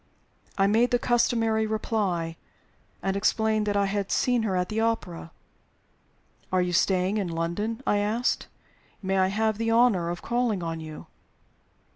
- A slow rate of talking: No, average, 155 wpm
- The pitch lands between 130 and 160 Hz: No, high, 205 Hz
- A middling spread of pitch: Yes, average, 3.6 semitones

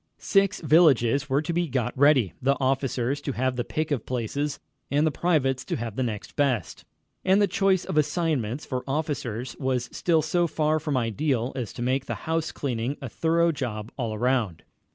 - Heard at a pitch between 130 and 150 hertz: Yes, low, 135 Hz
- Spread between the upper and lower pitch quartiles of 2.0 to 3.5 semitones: No, average, 4.1 semitones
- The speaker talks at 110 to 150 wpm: No, average, 185 wpm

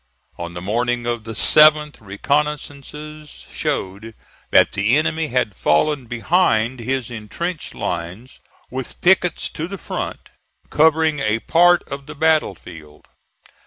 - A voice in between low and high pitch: No, low, 130 Hz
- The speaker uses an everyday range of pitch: No, wide, 6.0 semitones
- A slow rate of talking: Yes, slow, 125 wpm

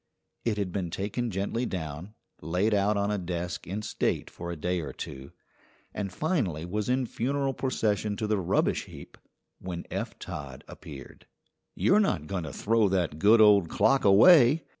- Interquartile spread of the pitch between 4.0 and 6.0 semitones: Yes, average, 4.4 semitones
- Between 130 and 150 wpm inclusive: No, average, 170 wpm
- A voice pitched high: No, low, 100 Hz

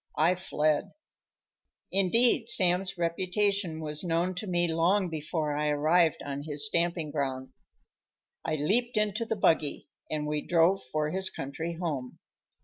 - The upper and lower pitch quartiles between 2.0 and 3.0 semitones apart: No, average, 3.7 semitones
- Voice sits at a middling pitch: Yes, medium, 170 Hz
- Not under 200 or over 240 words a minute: No, average, 140 wpm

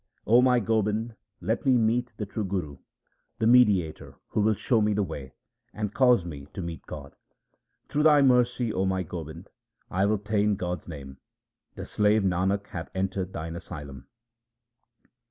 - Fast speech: No, average, 165 wpm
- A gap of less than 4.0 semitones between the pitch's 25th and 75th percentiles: No, average, 4.4 semitones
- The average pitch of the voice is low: Yes, low, 100 Hz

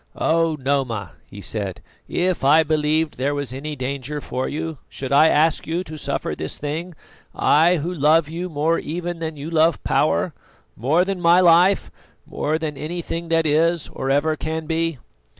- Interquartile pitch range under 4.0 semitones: Yes, narrow, 2.5 semitones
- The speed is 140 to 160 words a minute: No, average, 175 wpm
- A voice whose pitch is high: No, medium, 155 Hz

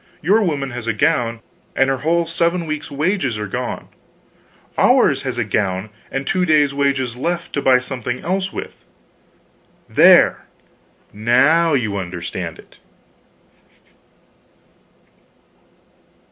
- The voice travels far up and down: Yes, wide, 6.0 semitones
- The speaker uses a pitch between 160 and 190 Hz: No, low, 135 Hz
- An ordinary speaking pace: No, slow, 120 wpm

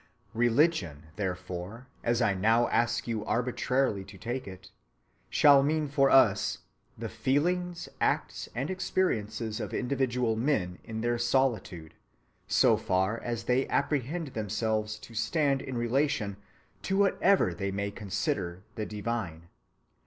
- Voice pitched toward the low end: Yes, low, 115 Hz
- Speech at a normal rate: No, slow, 130 wpm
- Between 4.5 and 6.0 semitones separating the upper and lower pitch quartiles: Yes, average, 4.9 semitones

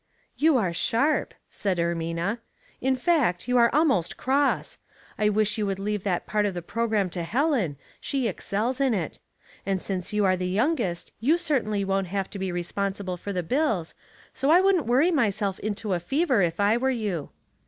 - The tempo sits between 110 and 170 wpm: No, average, 195 wpm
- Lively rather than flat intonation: Yes, wide, 5.8 semitones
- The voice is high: Yes, high, 210 Hz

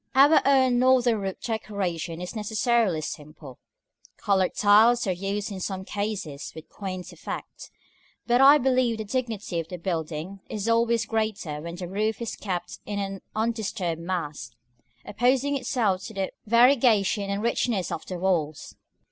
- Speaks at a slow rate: No, average, 155 wpm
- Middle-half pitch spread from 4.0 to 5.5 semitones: Yes, average, 4.5 semitones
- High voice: Yes, high, 205 Hz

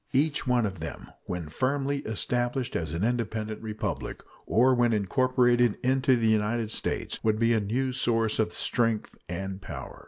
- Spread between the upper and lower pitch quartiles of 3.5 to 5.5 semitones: No, average, 3.0 semitones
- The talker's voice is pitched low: Yes, low, 115 Hz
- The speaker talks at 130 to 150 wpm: No, average, 160 wpm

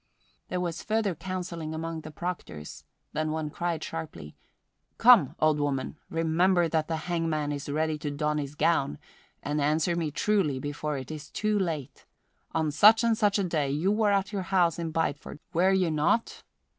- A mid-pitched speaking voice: Yes, medium, 160 Hz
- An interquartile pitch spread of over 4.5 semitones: No, average, 3.3 semitones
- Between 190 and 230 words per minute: No, average, 175 wpm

